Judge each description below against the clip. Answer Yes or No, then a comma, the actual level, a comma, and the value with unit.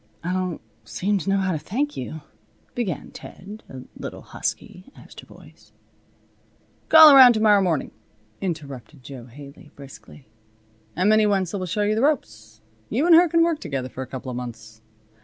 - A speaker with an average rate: Yes, average, 175 wpm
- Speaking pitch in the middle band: Yes, medium, 180 Hz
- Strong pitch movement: Yes, wide, 8.4 semitones